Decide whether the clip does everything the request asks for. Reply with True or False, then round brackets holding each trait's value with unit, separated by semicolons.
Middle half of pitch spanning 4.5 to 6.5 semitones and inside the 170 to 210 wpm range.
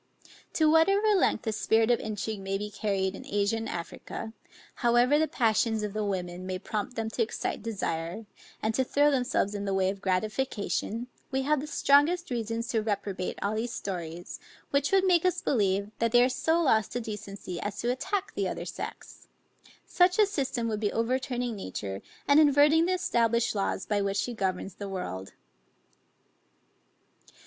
True (5.1 semitones; 175 wpm)